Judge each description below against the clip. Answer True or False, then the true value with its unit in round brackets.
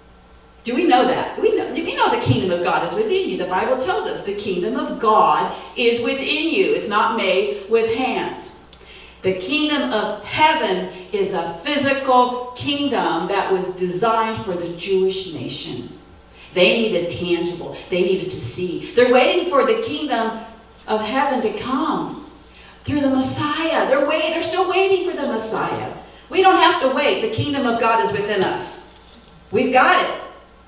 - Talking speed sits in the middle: True (170 wpm)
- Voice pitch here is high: True (250 Hz)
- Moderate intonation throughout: False (7.7 semitones)